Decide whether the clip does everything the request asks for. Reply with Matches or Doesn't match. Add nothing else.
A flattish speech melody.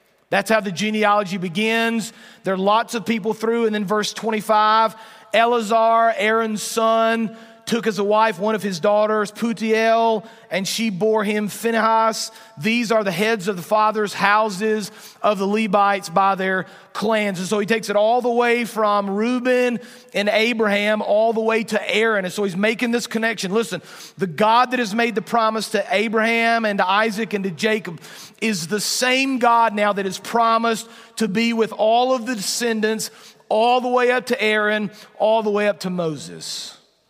Matches